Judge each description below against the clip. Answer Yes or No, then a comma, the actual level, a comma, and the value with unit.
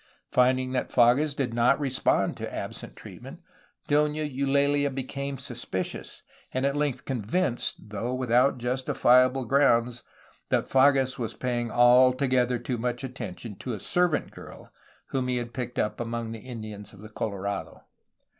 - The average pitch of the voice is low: Yes, low, 125 Hz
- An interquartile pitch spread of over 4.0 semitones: No, narrow, 2.5 semitones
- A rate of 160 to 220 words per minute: No, average, 145 wpm